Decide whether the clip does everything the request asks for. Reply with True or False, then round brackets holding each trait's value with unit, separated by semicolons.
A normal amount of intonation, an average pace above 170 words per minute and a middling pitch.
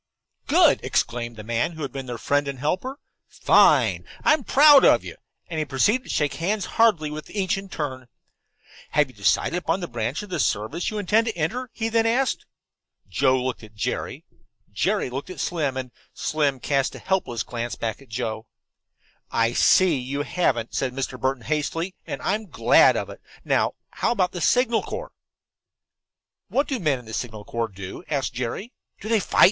False (7.8 semitones; 185 wpm; 150 Hz)